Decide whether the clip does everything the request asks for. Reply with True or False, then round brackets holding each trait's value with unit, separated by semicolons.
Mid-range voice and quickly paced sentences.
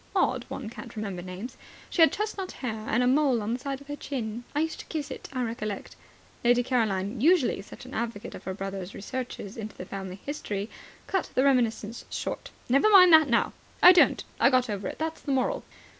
False (245 Hz; 215 wpm)